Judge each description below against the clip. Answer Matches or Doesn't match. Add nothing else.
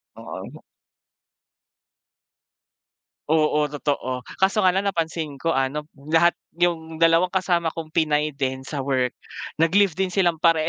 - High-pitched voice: Doesn't match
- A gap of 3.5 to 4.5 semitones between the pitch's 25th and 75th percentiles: Doesn't match